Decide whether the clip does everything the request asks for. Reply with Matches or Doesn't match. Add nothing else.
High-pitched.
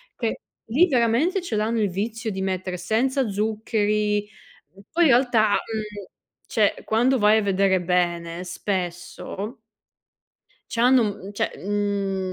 Matches